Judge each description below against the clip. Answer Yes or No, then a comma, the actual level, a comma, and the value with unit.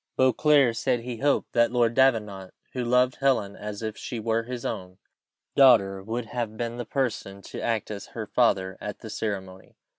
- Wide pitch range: No, average, 3.3 semitones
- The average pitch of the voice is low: Yes, low, 115 Hz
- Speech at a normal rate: Yes, average, 185 wpm